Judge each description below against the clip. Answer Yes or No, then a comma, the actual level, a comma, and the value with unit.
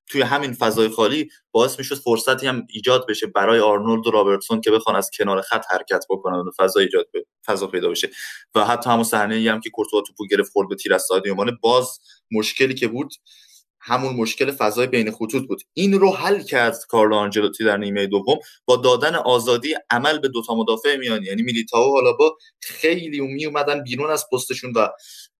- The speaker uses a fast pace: Yes, fast, 190 wpm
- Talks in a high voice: No, low, 125 Hz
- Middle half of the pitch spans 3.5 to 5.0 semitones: No, wide, 5.5 semitones